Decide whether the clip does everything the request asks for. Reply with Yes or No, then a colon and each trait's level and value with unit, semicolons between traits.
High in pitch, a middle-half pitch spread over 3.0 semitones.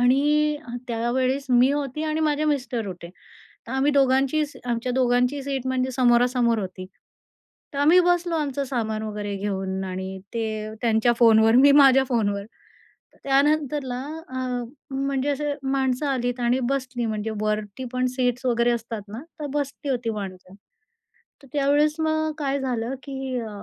Yes: very high, 255 Hz; average, 3.6 semitones